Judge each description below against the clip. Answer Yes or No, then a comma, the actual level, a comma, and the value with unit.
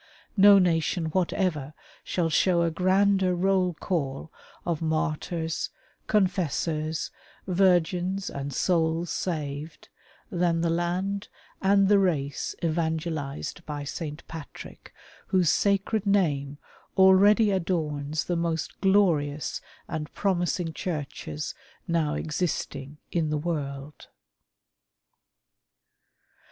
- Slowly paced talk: Yes, slow, 95 wpm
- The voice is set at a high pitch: No, medium, 170 Hz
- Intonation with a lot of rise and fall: No, average, 3.6 semitones